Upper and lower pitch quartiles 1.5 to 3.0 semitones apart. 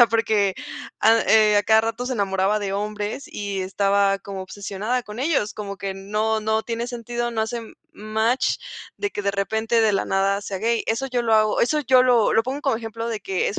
Yes: narrow, 2.6 semitones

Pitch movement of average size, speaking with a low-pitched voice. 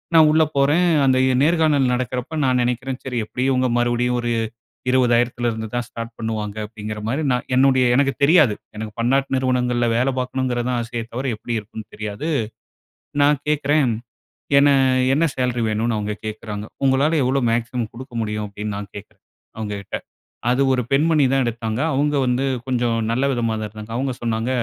Yes: average, 3.0 semitones; low, 125 Hz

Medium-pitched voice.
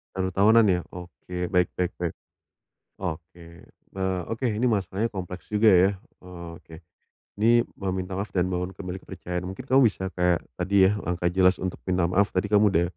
No: very low, 95 Hz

